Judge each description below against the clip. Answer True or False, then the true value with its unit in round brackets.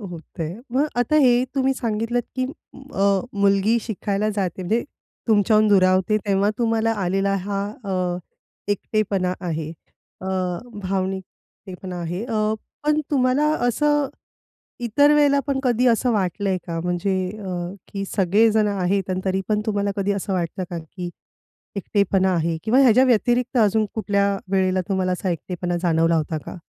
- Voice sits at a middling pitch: False (200 Hz)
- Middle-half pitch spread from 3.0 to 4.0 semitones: True (3.5 semitones)